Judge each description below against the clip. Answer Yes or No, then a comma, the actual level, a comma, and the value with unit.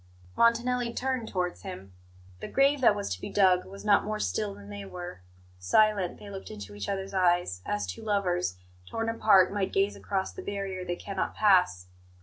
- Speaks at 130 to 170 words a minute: No, average, 185 wpm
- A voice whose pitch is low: No, high, 190 Hz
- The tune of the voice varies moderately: No, wide, 7.0 semitones